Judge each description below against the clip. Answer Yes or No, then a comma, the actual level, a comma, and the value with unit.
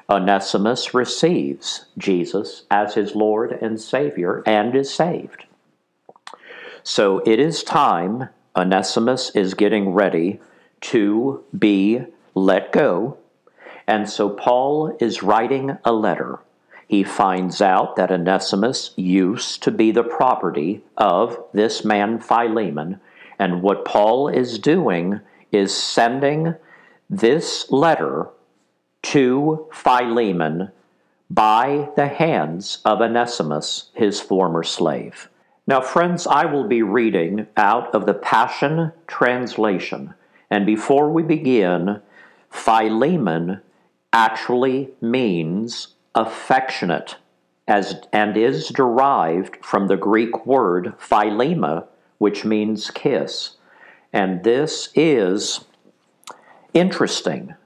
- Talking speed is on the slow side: Yes, slow, 100 wpm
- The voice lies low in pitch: Yes, low, 110 Hz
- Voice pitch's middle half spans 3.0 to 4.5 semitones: No, average, 4.9 semitones